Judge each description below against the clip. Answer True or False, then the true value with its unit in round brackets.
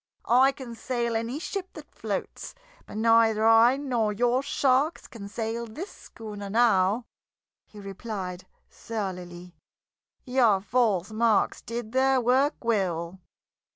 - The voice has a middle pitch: False (230 Hz)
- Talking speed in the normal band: False (120 wpm)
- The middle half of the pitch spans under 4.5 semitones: True (3.7 semitones)